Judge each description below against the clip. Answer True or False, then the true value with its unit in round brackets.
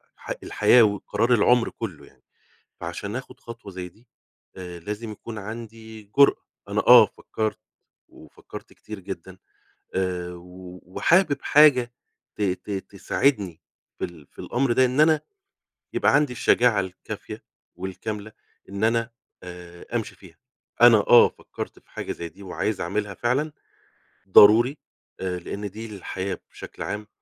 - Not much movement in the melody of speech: False (4.2 semitones)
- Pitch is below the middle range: True (105 Hz)